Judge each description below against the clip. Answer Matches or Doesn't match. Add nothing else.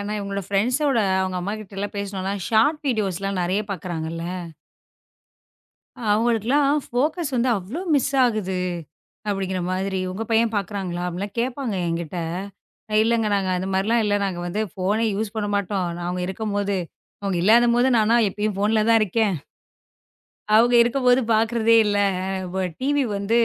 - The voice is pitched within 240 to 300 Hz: Doesn't match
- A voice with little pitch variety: Doesn't match